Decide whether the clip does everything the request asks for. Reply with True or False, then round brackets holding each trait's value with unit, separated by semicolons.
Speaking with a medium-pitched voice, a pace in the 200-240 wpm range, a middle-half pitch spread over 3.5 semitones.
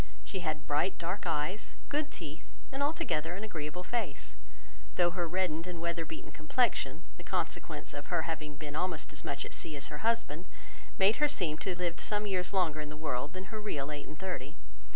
True (170 Hz; 205 wpm; 3.9 semitones)